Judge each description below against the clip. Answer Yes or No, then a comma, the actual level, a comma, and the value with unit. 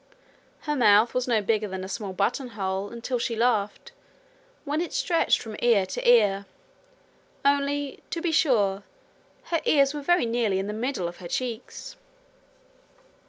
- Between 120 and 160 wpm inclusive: Yes, average, 155 wpm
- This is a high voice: Yes, high, 235 Hz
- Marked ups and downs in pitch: Yes, wide, 5.7 semitones